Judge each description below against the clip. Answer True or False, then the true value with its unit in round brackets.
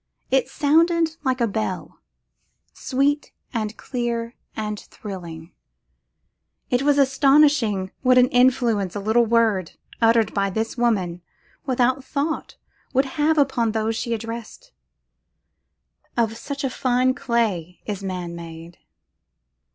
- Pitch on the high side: True (235 Hz)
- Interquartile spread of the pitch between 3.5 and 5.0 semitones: True (4.5 semitones)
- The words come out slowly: True (110 wpm)